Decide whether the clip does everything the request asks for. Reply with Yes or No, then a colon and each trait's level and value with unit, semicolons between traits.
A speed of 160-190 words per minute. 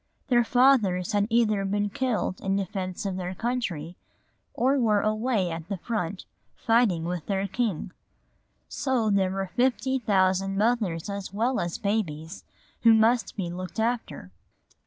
No: average, 145 wpm